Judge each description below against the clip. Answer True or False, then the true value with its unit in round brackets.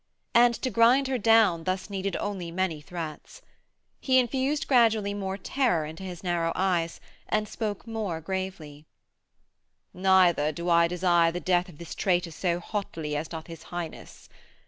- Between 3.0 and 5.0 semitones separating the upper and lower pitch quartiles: True (4.1 semitones)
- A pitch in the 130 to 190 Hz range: True (185 Hz)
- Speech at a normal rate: True (155 wpm)